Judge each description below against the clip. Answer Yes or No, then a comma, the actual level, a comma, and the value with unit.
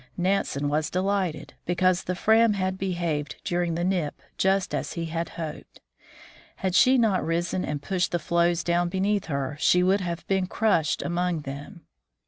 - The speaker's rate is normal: Yes, average, 165 wpm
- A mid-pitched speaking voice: Yes, medium, 175 Hz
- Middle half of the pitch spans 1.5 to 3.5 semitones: Yes, narrow, 2.5 semitones